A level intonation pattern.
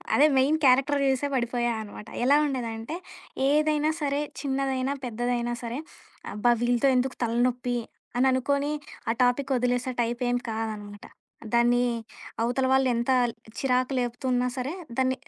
Yes: narrow, 2.0 semitones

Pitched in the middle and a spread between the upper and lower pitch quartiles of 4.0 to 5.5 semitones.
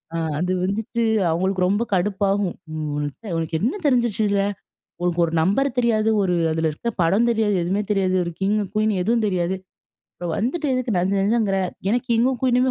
No: high, 205 Hz; average, 4.3 semitones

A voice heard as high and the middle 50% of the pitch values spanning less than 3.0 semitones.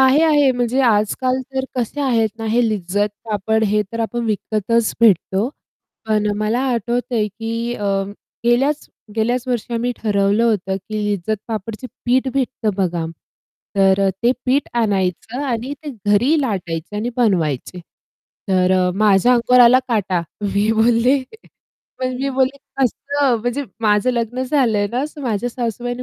No: high, 230 Hz; average, 3.4 semitones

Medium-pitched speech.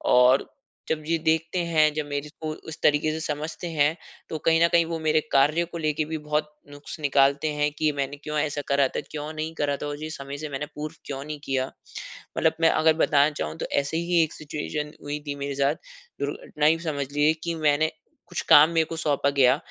Yes: medium, 150 Hz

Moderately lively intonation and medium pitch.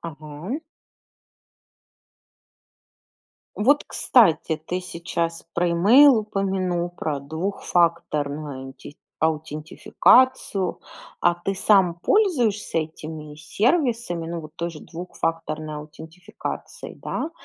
Yes: average, 4.2 semitones; medium, 170 Hz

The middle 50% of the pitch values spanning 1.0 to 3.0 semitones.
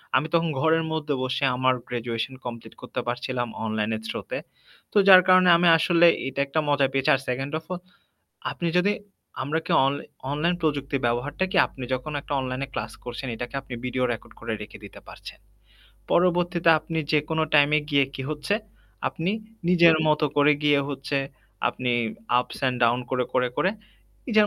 No: average, 4.3 semitones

